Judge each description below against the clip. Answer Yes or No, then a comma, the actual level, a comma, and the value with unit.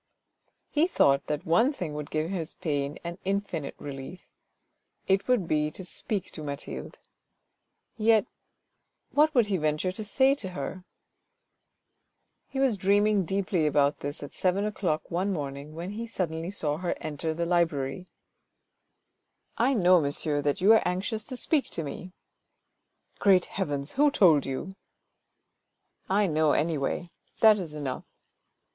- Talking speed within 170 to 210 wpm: No, average, 150 wpm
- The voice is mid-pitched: Yes, medium, 175 Hz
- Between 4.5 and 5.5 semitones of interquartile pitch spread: Yes, average, 5.1 semitones